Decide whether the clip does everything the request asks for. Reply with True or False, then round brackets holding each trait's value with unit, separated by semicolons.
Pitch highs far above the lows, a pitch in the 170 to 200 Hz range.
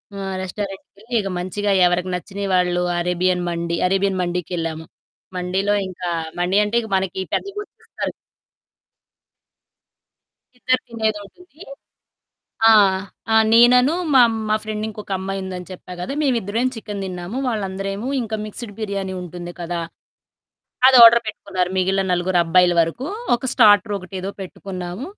False (3.3 semitones; 195 Hz)